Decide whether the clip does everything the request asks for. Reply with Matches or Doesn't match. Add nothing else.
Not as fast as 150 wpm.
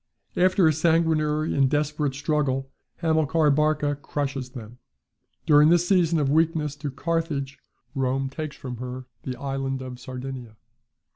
Matches